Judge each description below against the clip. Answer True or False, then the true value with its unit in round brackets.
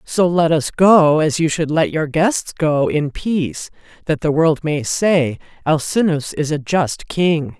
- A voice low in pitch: False (160 Hz)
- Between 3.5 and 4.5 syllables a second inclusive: True (3.8 syllables/s)